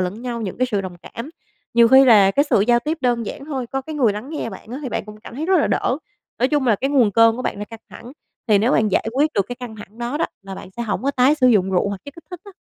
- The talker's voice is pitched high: Yes, high, 240 Hz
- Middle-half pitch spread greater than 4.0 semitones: Yes, average, 4.4 semitones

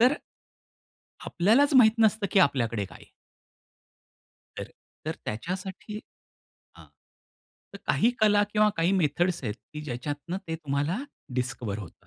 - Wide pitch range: Yes, wide, 7.6 semitones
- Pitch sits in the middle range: Yes, medium, 170 Hz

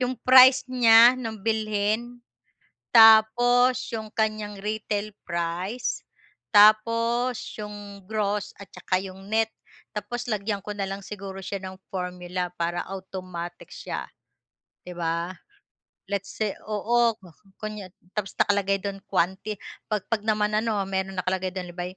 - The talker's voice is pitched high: Yes, high, 205 Hz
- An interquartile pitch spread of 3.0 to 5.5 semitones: No, narrow, 2.6 semitones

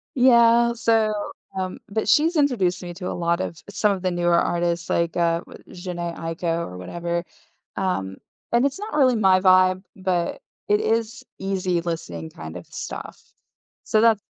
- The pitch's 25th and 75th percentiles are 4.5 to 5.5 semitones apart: Yes, average, 5.0 semitones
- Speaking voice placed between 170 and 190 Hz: Yes, medium, 185 Hz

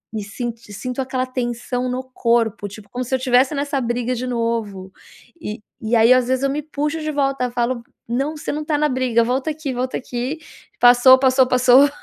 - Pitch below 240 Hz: No, very high, 255 Hz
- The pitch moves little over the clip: Yes, narrow, 2.1 semitones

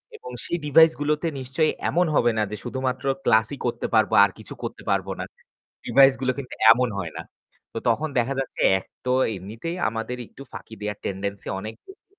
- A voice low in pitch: Yes, low, 125 Hz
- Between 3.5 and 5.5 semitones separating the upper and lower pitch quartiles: Yes, average, 5.0 semitones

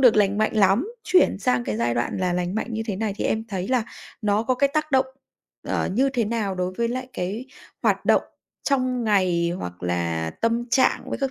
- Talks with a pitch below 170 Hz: No, high, 210 Hz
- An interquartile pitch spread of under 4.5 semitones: No, wide, 5.4 semitones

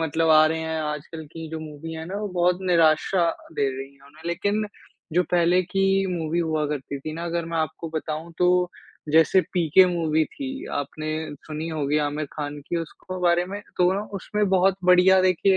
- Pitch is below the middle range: No, medium, 165 Hz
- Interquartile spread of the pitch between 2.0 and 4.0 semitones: Yes, narrow, 2.6 semitones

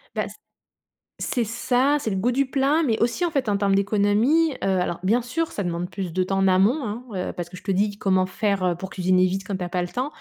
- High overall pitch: Yes, high, 200 Hz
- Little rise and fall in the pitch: No, average, 4.8 semitones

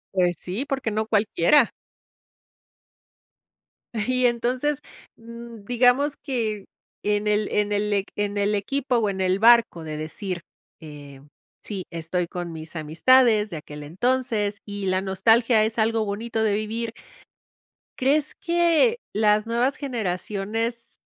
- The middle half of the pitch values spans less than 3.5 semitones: No, average, 3.8 semitones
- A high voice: Yes, high, 215 Hz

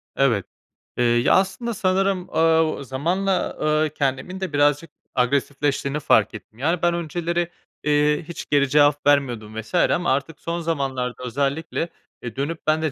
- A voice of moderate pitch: Yes, medium, 150 Hz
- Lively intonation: No, average, 3.9 semitones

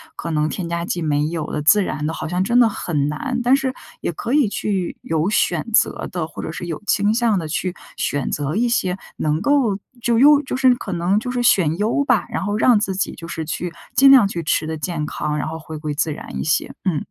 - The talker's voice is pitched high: No, medium, 180 Hz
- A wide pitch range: Yes, wide, 6.7 semitones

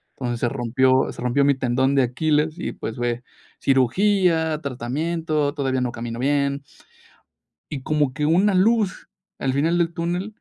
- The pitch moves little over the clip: No, average, 4.4 semitones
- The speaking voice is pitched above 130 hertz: Yes, medium, 140 Hz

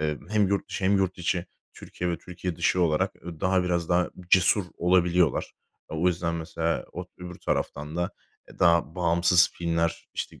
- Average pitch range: No, narrow, 1.5 semitones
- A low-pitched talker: Yes, very low, 85 Hz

